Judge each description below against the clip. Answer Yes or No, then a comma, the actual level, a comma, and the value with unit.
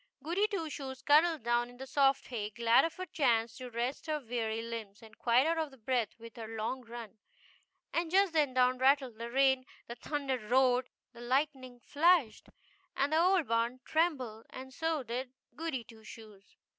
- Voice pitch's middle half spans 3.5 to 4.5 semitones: Yes, average, 4.2 semitones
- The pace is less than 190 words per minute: Yes, average, 180 wpm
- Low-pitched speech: No, very high, 255 Hz